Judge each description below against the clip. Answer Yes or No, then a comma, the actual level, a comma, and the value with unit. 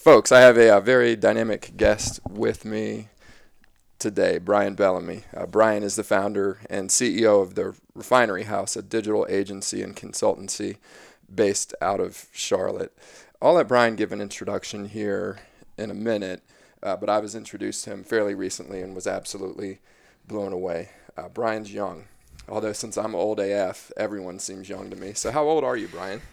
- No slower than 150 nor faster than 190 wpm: Yes, average, 175 wpm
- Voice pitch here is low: Yes, low, 105 Hz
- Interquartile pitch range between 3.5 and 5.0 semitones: No, average, 2.7 semitones